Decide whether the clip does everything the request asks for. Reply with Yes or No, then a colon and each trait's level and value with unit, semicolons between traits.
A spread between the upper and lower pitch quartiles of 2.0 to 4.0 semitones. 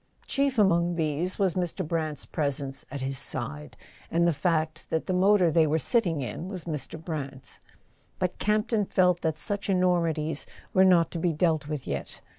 Yes: average, 3.2 semitones